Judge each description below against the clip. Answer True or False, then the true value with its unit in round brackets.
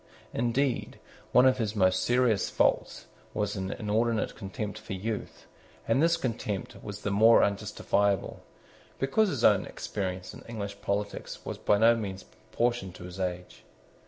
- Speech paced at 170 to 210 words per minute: False (150 wpm)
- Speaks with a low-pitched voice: True (105 Hz)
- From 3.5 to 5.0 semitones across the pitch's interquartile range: False (2.9 semitones)